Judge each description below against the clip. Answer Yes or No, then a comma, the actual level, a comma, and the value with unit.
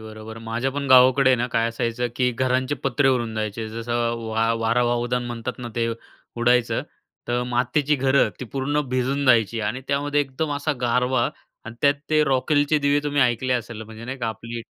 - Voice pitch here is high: No, low, 125 Hz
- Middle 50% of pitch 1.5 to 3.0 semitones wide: Yes, narrow, 2.6 semitones